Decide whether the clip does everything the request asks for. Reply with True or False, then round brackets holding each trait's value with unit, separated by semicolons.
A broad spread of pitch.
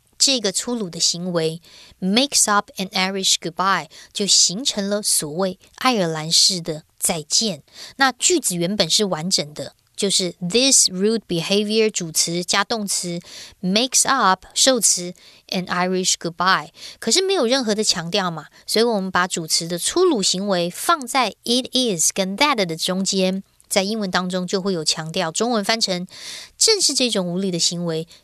False (3.9 semitones)